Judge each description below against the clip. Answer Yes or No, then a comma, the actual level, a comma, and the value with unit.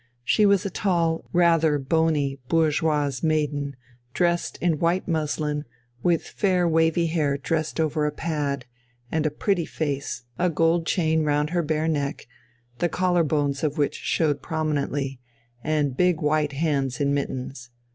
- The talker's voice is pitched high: No, medium, 155 Hz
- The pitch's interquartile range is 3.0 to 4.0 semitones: No, narrow, 2.5 semitones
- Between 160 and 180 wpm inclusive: No, average, 145 wpm